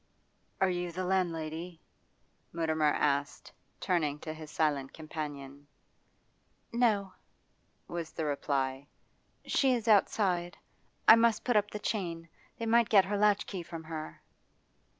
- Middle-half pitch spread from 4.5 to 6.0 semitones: Yes, average, 4.8 semitones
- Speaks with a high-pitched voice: No, medium, 170 Hz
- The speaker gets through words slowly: Yes, slow, 125 wpm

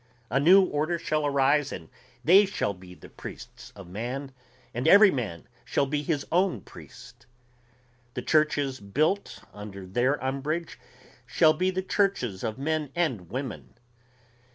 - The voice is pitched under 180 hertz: Yes, medium, 140 Hz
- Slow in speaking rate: No, average, 145 wpm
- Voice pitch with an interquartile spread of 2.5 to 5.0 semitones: No, wide, 5.6 semitones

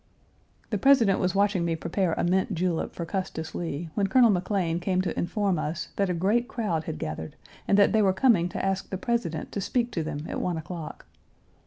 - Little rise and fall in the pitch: No, average, 3.3 semitones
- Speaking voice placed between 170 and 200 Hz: Yes, medium, 185 Hz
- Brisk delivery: Yes, fast, 210 wpm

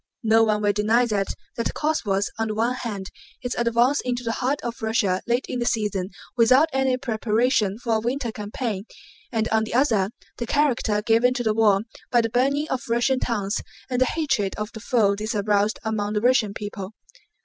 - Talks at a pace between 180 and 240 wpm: Yes, average, 200 wpm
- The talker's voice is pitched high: Yes, high, 225 Hz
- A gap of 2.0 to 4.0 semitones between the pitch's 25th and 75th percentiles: Yes, average, 2.9 semitones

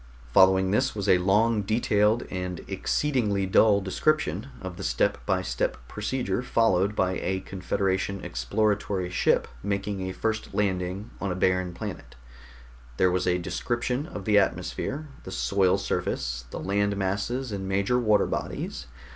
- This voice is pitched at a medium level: No, low, 100 Hz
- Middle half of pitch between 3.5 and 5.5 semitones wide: No, narrow, 2.5 semitones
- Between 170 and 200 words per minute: No, average, 145 wpm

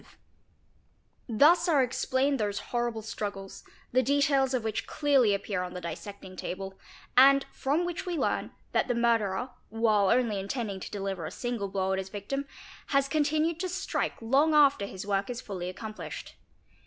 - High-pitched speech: Yes, high, 235 Hz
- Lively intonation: Yes, wide, 5.8 semitones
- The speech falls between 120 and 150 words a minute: No, average, 165 wpm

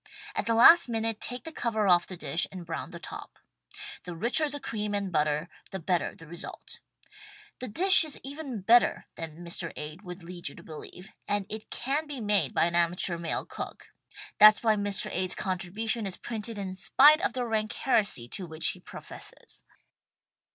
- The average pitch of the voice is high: Yes, high, 205 Hz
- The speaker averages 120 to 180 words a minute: No, average, 190 wpm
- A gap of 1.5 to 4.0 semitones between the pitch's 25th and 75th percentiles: No, average, 5.3 semitones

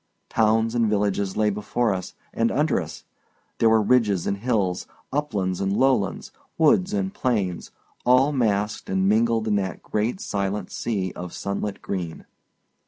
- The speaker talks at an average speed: Yes, average, 150 wpm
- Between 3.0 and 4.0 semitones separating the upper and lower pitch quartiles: Yes, average, 3.6 semitones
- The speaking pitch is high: No, low, 105 Hz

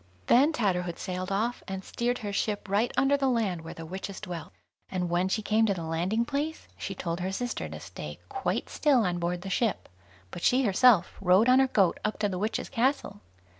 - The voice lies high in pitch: Yes, high, 200 Hz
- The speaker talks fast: Yes, fast, 210 wpm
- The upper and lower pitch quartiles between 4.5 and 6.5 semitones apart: Yes, average, 5.1 semitones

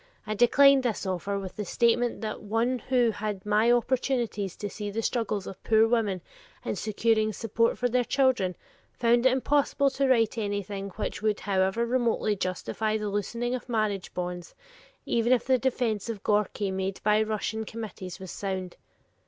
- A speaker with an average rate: Yes, average, 170 wpm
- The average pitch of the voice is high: Yes, high, 220 Hz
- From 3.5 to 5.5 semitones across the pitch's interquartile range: No, average, 3.1 semitones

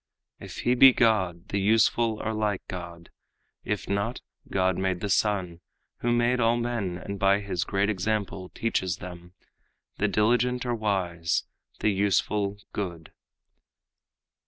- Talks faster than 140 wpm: No, slow, 135 wpm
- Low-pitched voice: Yes, low, 100 Hz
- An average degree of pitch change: Yes, average, 3.3 semitones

